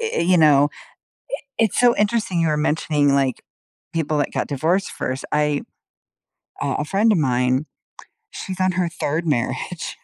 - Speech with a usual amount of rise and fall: Yes, average, 4.4 semitones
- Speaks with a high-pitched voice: No, medium, 155 Hz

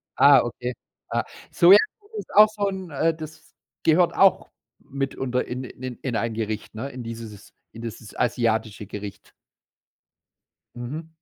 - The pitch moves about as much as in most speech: No, wide, 6.1 semitones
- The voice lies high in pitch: No, low, 125 Hz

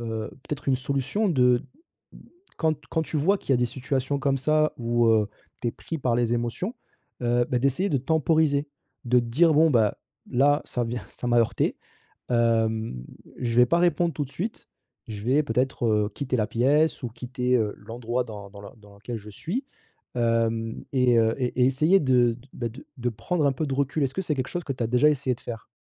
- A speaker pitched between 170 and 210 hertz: No, low, 125 Hz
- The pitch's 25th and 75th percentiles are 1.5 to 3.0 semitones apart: No, average, 3.7 semitones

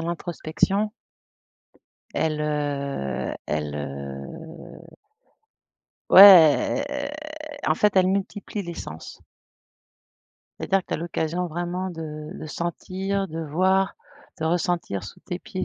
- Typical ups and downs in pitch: Yes, average, 3.8 semitones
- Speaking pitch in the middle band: Yes, medium, 170 Hz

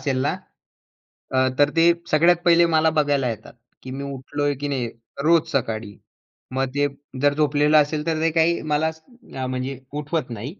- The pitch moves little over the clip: No, average, 3.2 semitones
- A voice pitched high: No, medium, 145 Hz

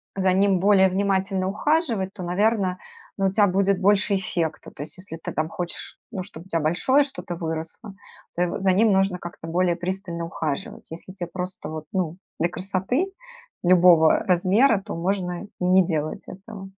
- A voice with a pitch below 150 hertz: No, medium, 185 Hz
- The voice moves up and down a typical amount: No, narrow, 2.3 semitones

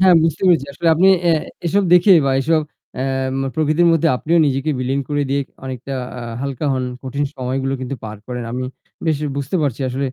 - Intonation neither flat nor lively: Yes, average, 3.5 semitones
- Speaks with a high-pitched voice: No, medium, 140 Hz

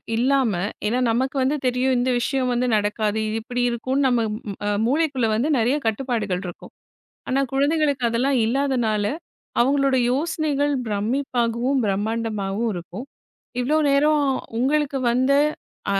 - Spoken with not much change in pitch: No, average, 3.6 semitones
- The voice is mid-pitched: No, very high, 250 Hz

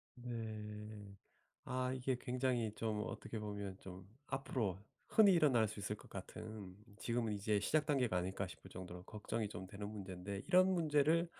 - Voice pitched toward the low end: Yes, low, 110 Hz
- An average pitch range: Yes, average, 4.4 semitones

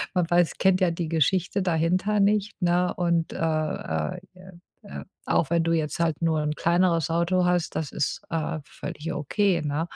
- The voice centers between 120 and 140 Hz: No, medium, 170 Hz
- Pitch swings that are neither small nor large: No, narrow, 2.2 semitones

